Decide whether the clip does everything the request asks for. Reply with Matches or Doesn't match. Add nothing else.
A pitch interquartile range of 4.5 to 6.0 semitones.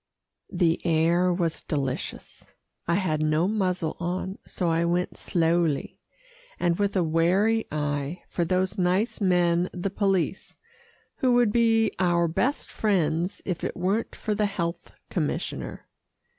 Doesn't match